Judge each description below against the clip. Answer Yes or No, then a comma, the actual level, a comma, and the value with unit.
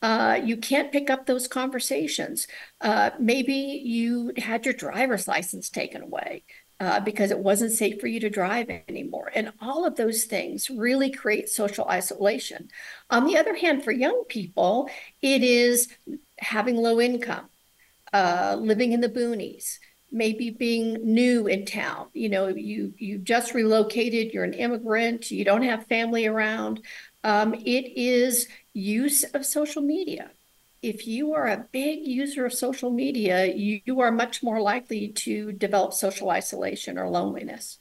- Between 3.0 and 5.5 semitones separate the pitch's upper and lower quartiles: Yes, average, 3.3 semitones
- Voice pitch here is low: No, high, 235 Hz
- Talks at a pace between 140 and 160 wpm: Yes, average, 155 wpm